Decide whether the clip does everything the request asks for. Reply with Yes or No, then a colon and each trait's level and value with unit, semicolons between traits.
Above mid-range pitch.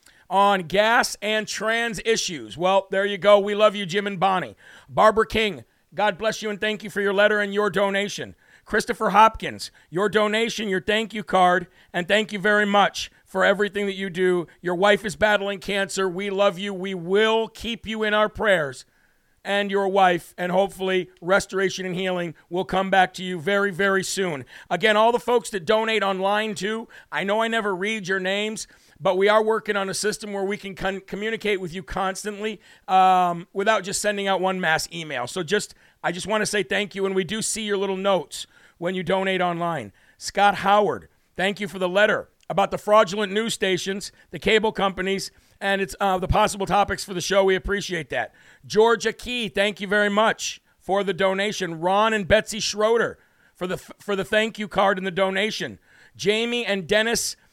Yes: high, 200 Hz